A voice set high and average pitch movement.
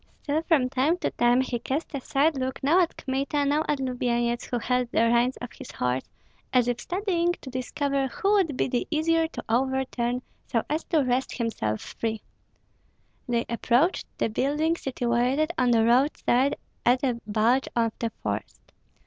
Yes: very high, 255 Hz; average, 3.5 semitones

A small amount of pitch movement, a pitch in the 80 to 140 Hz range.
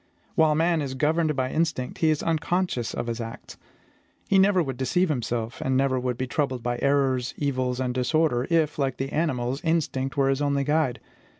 No: average, 3.7 semitones; low, 135 Hz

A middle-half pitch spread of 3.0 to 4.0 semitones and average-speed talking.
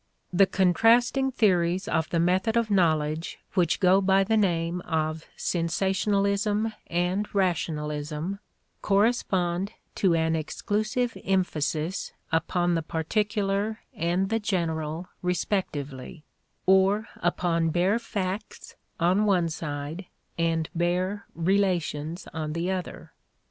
No: average, 3.4 semitones; slow, 105 wpm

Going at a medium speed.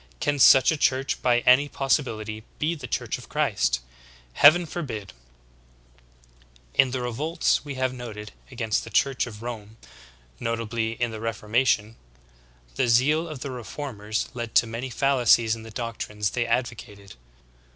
Yes: average, 150 wpm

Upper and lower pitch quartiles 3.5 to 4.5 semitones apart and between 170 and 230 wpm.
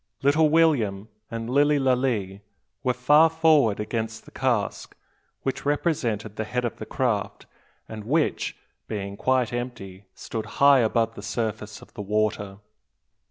No: average, 4.2 semitones; average, 140 wpm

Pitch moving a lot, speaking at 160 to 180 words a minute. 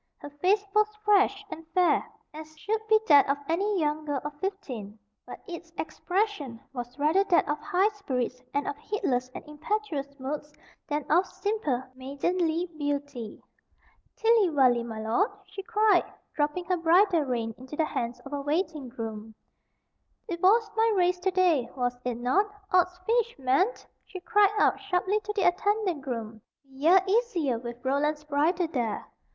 Yes: wide, 6.4 semitones; average, 165 wpm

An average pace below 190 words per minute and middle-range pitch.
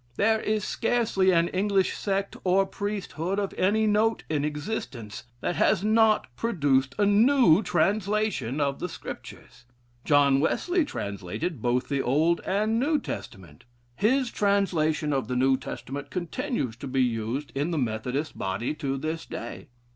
Yes: average, 145 wpm; medium, 170 Hz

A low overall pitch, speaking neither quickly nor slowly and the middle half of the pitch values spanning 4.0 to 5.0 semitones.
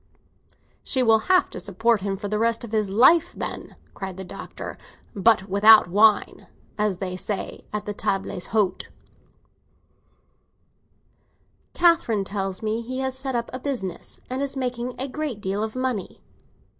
No: high, 220 Hz; average, 155 wpm; average, 4.4 semitones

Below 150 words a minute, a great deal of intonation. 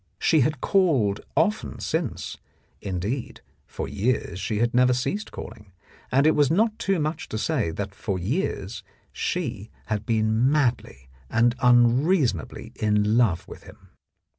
Yes: average, 140 wpm; wide, 6.3 semitones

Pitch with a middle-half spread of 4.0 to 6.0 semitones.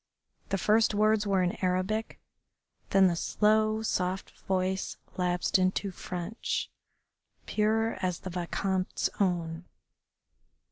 No: average, 2.8 semitones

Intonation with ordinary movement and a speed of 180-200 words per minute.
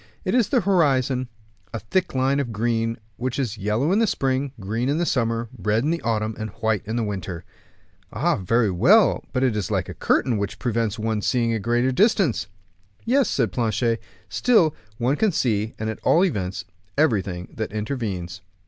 Yes: average, 4.4 semitones; average, 185 wpm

